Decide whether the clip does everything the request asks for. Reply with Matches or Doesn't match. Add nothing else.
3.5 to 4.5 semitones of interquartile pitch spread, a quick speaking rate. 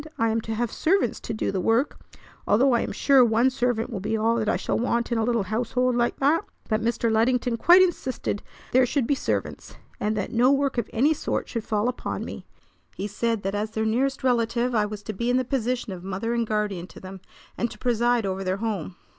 Doesn't match